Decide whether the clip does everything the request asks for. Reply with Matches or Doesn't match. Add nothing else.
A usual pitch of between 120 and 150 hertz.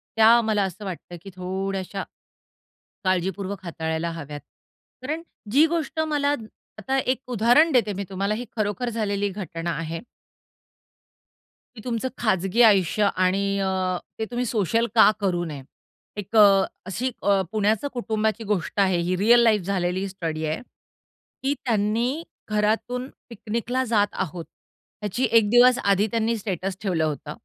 Doesn't match